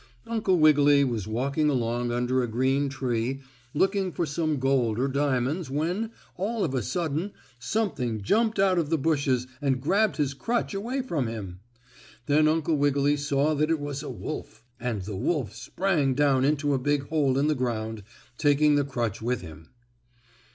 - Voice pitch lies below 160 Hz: Yes, medium, 140 Hz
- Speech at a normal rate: Yes, average, 170 wpm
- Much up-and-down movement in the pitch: No, average, 4.0 semitones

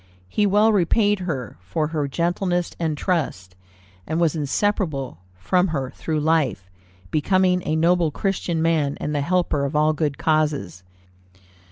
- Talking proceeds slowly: No, average, 145 wpm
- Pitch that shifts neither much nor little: Yes, average, 3.8 semitones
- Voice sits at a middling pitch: Yes, medium, 160 Hz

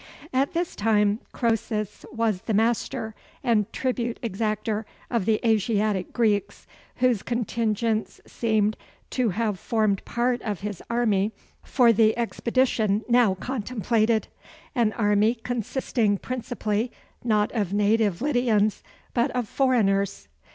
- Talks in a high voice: Yes, high, 220 Hz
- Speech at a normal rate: No, slow, 115 wpm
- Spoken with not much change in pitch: Yes, narrow, 2.3 semitones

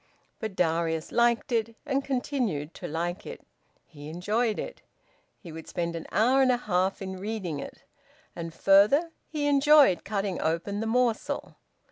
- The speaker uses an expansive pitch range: Yes, wide, 6.5 semitones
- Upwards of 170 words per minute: No, average, 155 wpm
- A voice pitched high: Yes, high, 205 Hz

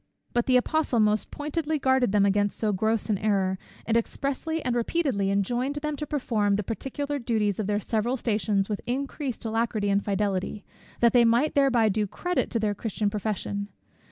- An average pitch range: Yes, average, 4.3 semitones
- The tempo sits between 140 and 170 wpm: No, average, 180 wpm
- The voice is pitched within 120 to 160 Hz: No, high, 225 Hz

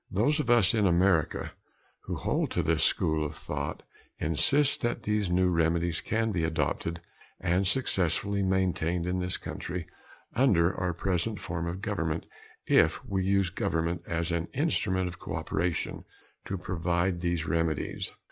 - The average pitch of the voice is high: No, very low, 90 Hz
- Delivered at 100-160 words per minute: Yes, average, 145 wpm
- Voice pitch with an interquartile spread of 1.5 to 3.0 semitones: Yes, average, 2.7 semitones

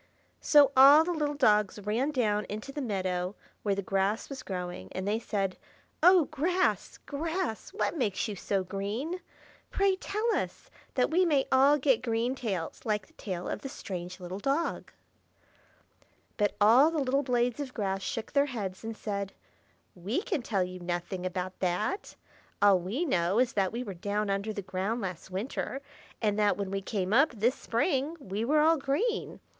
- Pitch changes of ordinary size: No, wide, 6.4 semitones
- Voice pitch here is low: No, high, 220 Hz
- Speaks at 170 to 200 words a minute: Yes, average, 180 wpm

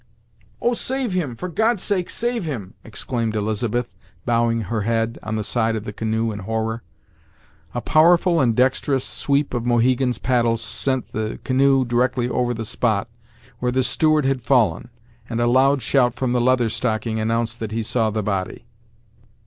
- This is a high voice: No, low, 120 Hz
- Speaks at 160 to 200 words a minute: Yes, average, 170 wpm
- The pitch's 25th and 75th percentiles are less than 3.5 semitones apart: Yes, average, 2.9 semitones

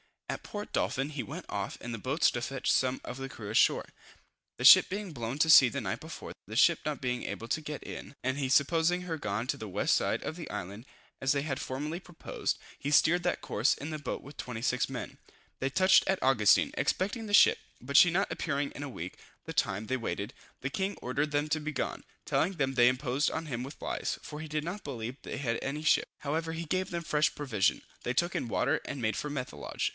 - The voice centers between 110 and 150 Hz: Yes, medium, 140 Hz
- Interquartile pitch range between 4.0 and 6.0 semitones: Yes, average, 4.4 semitones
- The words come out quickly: Yes, fast, 235 wpm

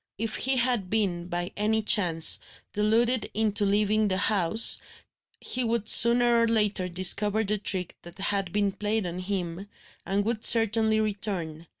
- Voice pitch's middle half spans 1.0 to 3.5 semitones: Yes, average, 2.9 semitones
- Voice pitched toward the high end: Yes, high, 210 Hz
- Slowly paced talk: No, average, 155 wpm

